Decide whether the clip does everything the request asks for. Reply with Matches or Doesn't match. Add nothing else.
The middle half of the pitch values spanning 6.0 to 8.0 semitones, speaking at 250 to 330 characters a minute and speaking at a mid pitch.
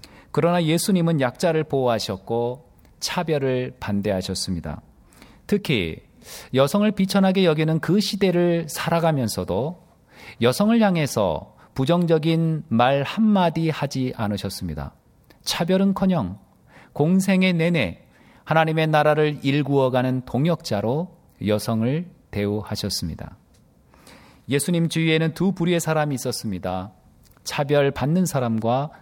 Matches